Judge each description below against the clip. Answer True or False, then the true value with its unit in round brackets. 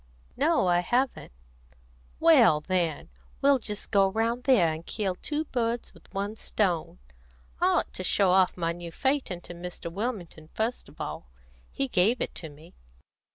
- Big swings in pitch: True (5.7 semitones)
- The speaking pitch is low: False (195 Hz)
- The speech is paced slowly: False (160 wpm)